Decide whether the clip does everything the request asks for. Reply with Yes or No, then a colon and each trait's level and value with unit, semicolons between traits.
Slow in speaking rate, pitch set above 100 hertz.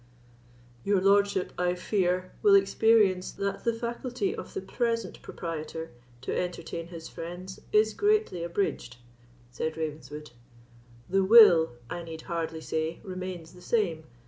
Yes: slow, 130 wpm; medium, 185 Hz